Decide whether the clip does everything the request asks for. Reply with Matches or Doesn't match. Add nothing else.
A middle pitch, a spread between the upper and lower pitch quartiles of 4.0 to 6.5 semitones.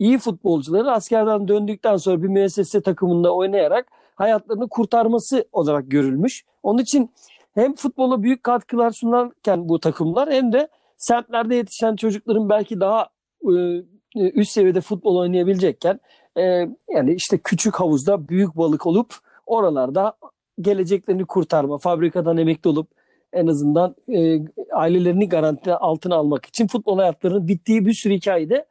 Doesn't match